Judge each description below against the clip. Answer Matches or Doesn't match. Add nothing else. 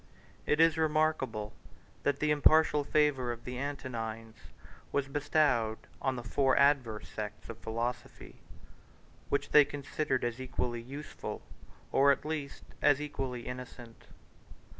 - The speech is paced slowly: Matches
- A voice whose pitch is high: Doesn't match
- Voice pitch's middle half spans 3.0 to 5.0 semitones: Matches